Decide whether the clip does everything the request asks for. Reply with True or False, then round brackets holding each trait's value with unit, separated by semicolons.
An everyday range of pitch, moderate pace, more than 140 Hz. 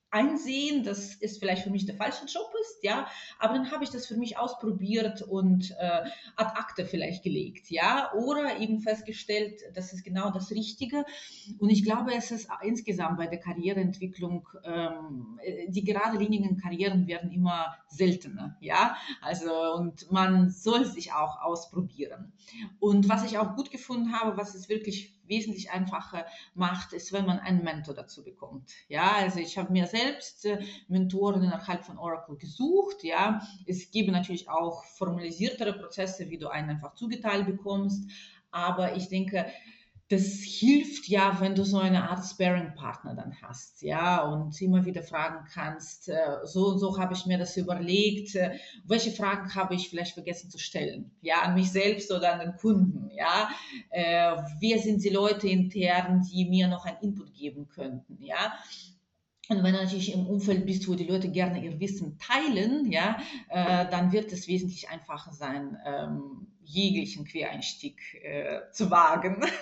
True (3.2 semitones; 165 wpm; 190 Hz)